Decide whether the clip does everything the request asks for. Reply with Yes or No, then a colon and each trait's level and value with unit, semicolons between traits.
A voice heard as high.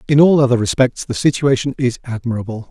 No: low, 125 Hz